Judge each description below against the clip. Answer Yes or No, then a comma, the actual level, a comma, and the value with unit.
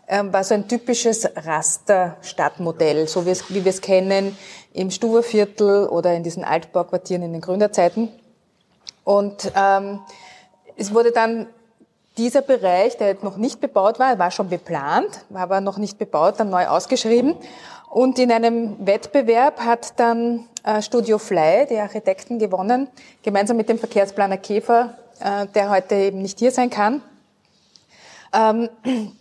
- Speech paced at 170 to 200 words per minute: No, average, 145 wpm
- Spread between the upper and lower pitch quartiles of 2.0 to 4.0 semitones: Yes, average, 3.5 semitones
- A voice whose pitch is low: No, high, 210 Hz